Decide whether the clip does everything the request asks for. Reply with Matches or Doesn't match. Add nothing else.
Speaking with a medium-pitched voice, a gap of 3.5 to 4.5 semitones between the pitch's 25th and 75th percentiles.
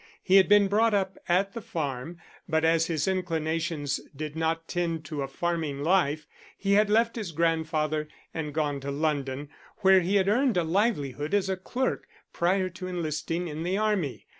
Matches